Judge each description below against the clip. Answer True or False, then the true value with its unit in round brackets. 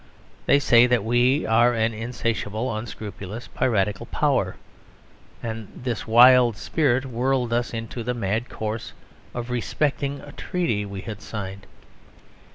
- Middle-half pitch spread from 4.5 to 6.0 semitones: False (2.4 semitones)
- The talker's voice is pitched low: True (115 Hz)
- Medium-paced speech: False (130 wpm)